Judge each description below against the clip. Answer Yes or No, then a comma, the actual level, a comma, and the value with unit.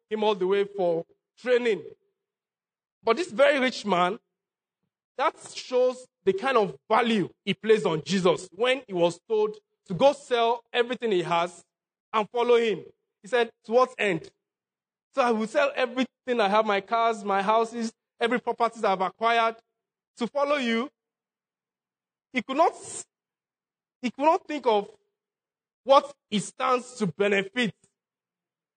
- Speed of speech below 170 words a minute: Yes, average, 150 wpm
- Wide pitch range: No, average, 4.3 semitones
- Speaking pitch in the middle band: No, high, 230 Hz